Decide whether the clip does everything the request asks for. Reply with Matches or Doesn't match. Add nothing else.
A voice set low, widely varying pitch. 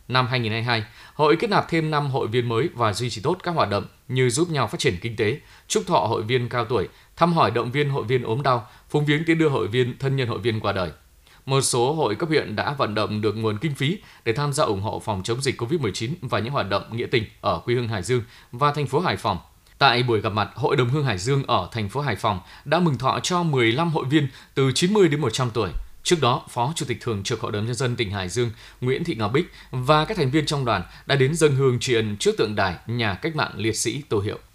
Doesn't match